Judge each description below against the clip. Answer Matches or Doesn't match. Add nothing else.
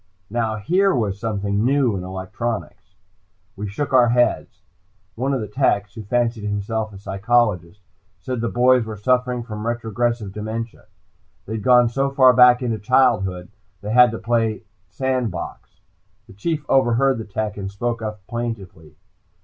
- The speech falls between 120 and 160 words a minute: Matches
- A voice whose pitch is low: Matches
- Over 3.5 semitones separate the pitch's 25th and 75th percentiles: Doesn't match